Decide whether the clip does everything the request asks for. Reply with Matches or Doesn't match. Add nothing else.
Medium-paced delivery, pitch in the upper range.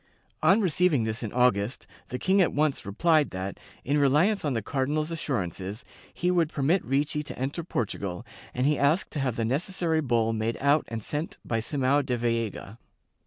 Doesn't match